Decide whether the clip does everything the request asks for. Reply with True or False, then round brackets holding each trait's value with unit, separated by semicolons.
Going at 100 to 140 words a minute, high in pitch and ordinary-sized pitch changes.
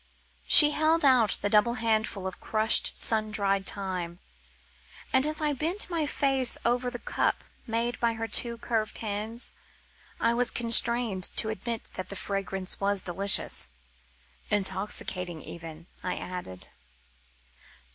True (135 wpm; 220 Hz; 3.7 semitones)